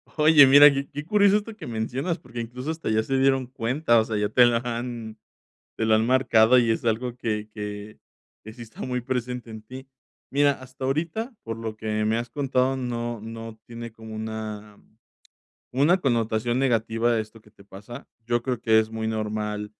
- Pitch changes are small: No, average, 3.1 semitones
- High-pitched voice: No, low, 120 Hz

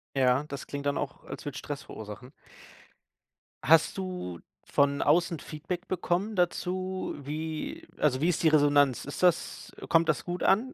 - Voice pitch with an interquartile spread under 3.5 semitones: No, average, 3.9 semitones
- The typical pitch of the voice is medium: Yes, medium, 155 Hz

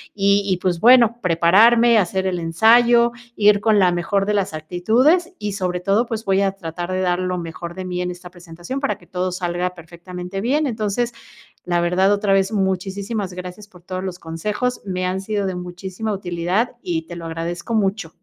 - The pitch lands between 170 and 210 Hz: Yes, high, 190 Hz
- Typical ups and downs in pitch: Yes, average, 3.0 semitones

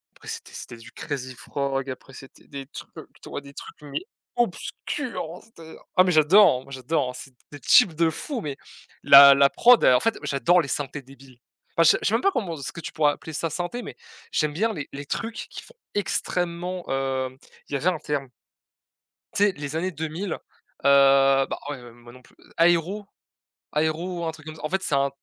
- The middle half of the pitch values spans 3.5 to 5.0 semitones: Yes, average, 4.7 semitones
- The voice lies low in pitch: No, medium, 155 Hz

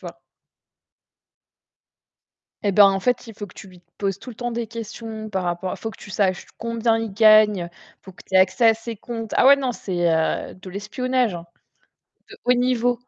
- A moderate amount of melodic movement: Yes, average, 3.4 semitones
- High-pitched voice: Yes, high, 215 Hz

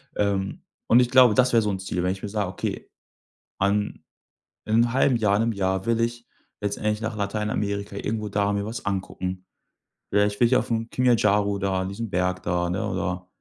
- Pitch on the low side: Yes, low, 105 Hz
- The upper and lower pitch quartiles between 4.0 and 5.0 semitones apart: No, average, 2.8 semitones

